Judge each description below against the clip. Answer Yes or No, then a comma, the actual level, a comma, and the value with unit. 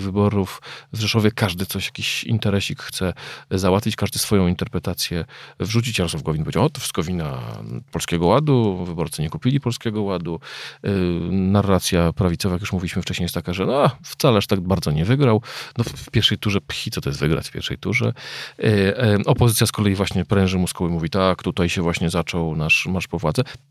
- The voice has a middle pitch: No, very low, 95 Hz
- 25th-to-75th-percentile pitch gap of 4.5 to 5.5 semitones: No, average, 3.5 semitones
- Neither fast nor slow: No, fast, 185 wpm